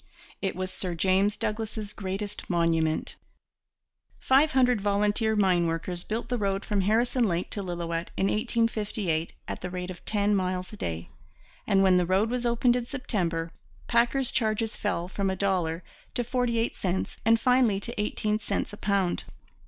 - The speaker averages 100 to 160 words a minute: No, average, 170 wpm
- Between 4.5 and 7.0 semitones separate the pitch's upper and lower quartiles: No, average, 3.8 semitones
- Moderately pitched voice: No, high, 200 Hz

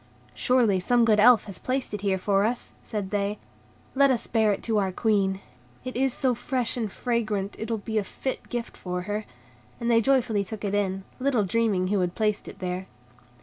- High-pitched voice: Yes, high, 215 Hz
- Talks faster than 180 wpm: Yes, fast, 205 wpm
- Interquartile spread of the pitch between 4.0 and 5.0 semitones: No, average, 3.3 semitones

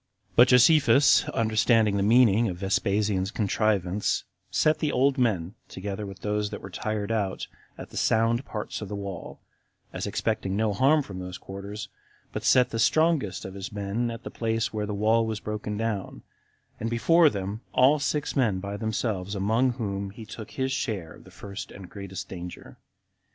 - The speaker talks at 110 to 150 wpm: No, average, 180 wpm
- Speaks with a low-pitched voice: Yes, low, 105 Hz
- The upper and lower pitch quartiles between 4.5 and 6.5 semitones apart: No, average, 3.0 semitones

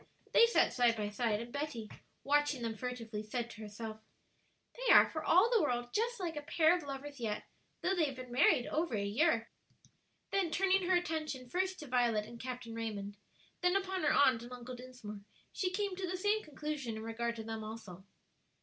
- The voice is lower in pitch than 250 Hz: No, very high, 255 Hz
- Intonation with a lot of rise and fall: Yes, wide, 7.3 semitones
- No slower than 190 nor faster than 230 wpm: Yes, average, 200 wpm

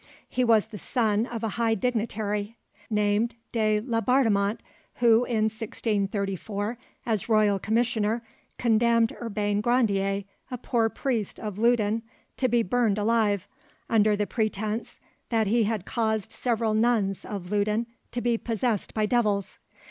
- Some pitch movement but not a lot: No, narrow, 2.2 semitones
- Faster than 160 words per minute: No, slow, 135 wpm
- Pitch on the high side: Yes, high, 220 Hz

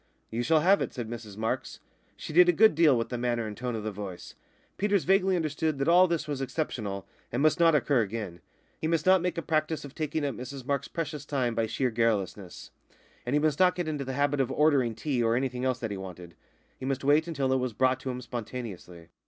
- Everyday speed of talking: No, fast, 240 wpm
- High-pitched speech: No, low, 130 Hz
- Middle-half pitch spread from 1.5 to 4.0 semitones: No, average, 5.1 semitones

